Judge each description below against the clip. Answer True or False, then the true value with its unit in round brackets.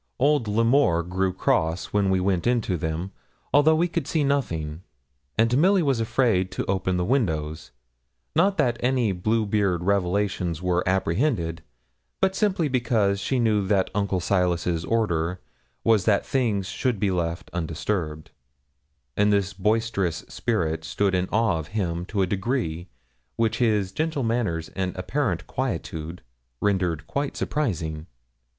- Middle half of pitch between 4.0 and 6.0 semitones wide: True (5.3 semitones)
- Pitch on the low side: True (100 Hz)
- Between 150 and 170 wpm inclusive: False (140 wpm)